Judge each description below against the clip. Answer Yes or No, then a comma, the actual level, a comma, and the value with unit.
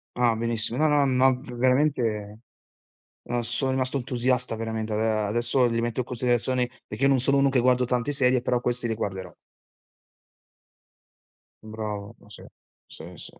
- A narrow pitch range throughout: Yes, narrow, 2.3 semitones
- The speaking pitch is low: Yes, low, 120 Hz